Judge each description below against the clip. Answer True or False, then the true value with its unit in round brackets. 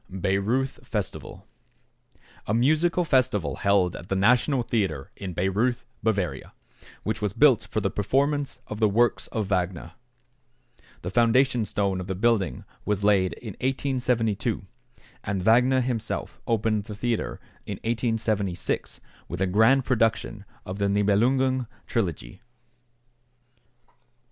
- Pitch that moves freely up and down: False (3.9 semitones)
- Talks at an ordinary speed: False (125 wpm)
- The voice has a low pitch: True (110 Hz)